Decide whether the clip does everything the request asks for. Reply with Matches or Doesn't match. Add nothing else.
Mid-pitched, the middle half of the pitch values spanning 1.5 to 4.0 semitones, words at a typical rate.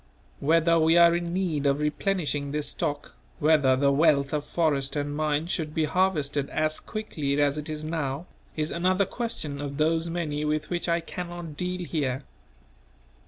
Matches